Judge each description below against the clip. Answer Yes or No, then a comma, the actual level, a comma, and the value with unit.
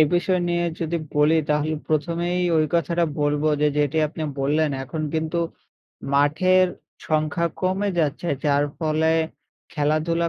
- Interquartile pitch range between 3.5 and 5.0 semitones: No, narrow, 2.4 semitones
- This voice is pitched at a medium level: Yes, medium, 155 Hz